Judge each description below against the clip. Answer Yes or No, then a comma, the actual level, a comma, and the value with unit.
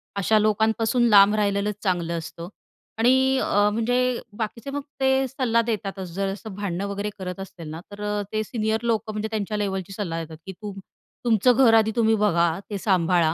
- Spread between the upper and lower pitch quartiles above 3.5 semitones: No, average, 2.7 semitones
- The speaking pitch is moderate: No, high, 210 Hz